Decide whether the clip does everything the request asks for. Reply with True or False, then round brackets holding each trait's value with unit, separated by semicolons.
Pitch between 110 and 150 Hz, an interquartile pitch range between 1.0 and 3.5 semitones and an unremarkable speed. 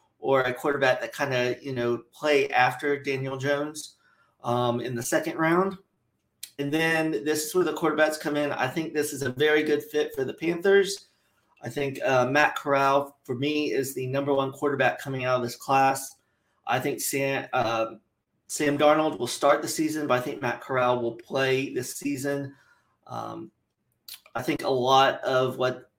True (140 Hz; 2.9 semitones; 185 wpm)